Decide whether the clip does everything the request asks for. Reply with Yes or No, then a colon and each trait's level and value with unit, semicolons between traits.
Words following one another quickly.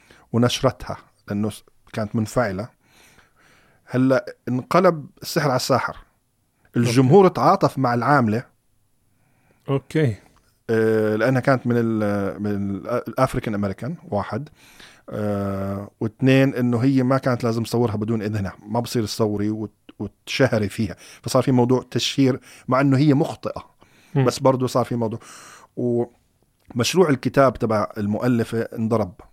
No: average, 110 wpm